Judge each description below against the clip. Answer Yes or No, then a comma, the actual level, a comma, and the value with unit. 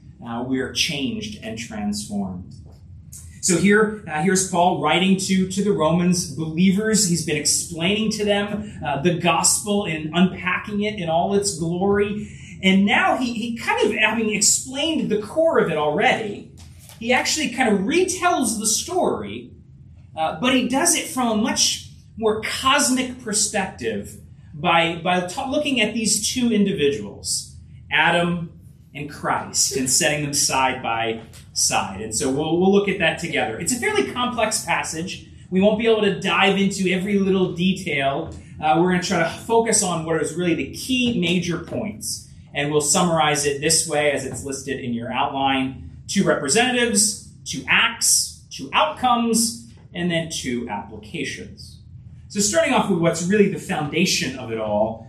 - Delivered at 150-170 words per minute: Yes, average, 165 wpm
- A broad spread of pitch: Yes, wide, 6.1 semitones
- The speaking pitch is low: No, medium, 180 Hz